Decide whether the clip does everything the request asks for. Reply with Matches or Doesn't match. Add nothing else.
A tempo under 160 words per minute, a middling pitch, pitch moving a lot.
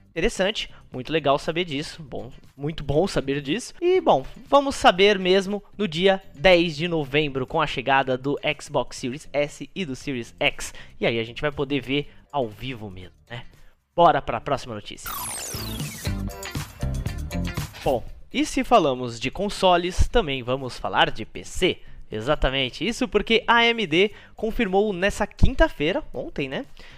Matches